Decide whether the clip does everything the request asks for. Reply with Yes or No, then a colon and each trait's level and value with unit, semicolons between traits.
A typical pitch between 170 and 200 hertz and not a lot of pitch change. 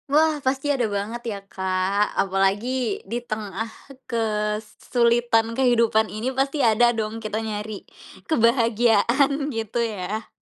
No: high, 225 Hz; narrow, 2.3 semitones